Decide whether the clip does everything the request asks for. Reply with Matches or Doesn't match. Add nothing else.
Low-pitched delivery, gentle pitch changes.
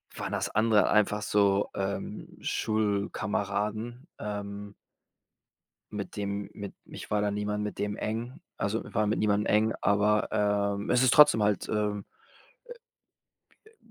Matches